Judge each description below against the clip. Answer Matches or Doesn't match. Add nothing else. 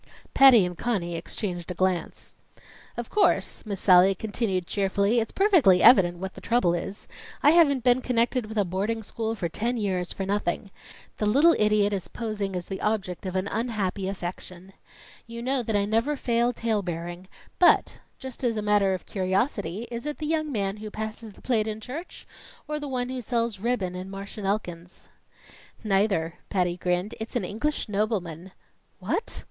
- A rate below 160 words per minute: Doesn't match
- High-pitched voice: Matches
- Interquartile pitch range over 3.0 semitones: Matches